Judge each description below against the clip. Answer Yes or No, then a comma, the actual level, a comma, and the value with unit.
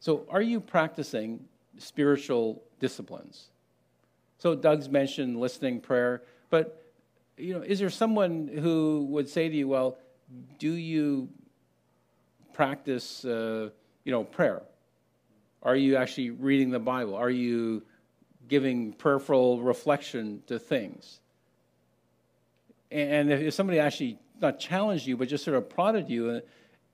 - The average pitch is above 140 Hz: No, low, 135 Hz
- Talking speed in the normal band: No, slow, 125 wpm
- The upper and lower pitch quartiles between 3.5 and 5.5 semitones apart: Yes, average, 4.2 semitones